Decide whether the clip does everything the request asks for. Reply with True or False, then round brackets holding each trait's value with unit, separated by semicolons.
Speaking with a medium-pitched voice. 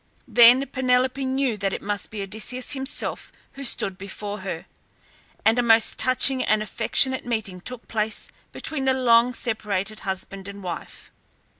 False (225 Hz)